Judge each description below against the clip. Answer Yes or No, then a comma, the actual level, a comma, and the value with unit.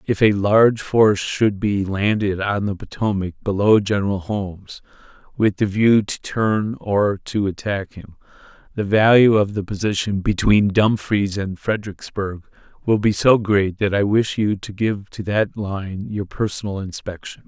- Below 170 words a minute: Yes, average, 160 wpm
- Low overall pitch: Yes, low, 100 Hz